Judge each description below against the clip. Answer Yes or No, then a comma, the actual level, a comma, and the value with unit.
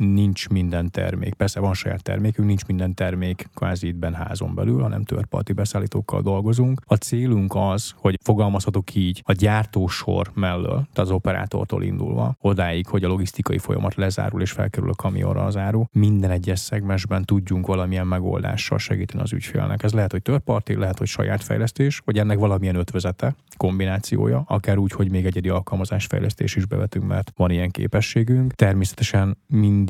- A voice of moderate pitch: No, low, 100 Hz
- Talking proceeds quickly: Yes, fast, 160 wpm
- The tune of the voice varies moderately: Yes, average, 3.1 semitones